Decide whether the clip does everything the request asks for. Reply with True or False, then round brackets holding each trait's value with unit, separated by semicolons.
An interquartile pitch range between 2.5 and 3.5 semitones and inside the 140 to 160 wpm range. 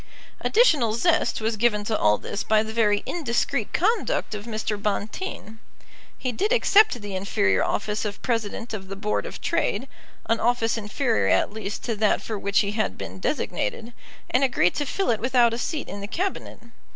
False (3.1 semitones; 185 wpm)